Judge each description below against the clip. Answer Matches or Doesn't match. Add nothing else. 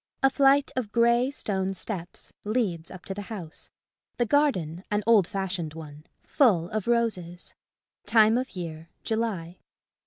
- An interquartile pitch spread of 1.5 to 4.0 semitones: Doesn't match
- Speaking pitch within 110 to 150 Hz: Doesn't match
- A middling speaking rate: Matches